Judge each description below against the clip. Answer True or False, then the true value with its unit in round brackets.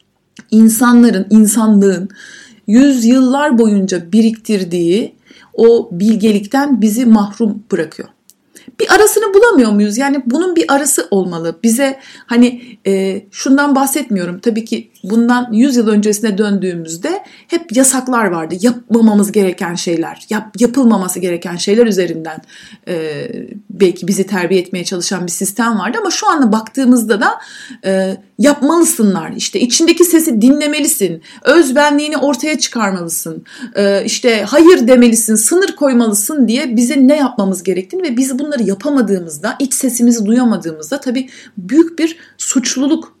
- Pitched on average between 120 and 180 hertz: False (230 Hz)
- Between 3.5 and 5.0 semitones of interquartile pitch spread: False (5.5 semitones)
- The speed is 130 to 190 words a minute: False (120 wpm)